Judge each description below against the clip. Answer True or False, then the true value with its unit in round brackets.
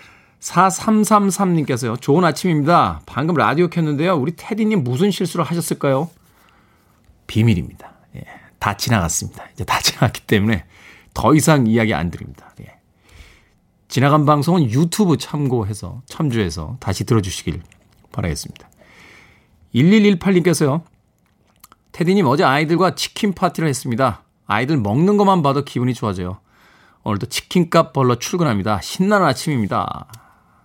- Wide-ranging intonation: True (8.4 semitones)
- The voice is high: False (140 Hz)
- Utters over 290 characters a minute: True (310 characters per minute)